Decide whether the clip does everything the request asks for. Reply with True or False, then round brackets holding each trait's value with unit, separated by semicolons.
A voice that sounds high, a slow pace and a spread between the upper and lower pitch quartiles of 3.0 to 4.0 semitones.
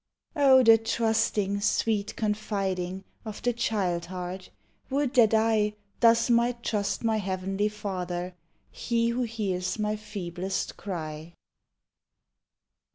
True (210 Hz; 110 wpm; 3.4 semitones)